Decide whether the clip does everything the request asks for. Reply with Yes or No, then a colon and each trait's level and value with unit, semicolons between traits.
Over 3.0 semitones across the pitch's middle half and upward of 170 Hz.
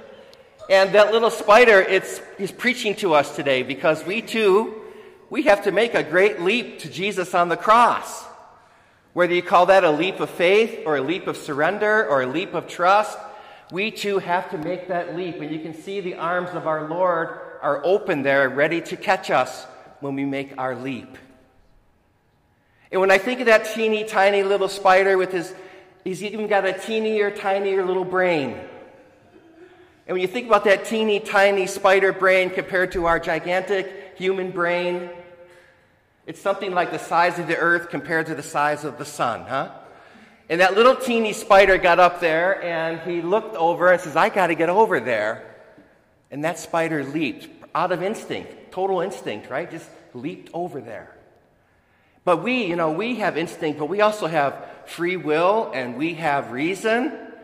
Yes: average, 3.7 semitones; medium, 185 Hz